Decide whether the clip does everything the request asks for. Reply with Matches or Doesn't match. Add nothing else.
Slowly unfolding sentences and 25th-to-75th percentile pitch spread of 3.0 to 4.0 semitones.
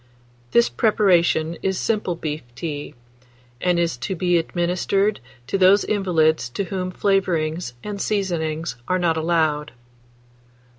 Matches